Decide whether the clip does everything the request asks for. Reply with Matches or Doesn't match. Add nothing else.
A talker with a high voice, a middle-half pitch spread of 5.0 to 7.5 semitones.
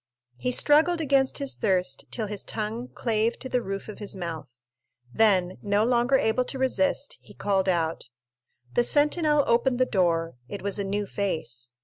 Matches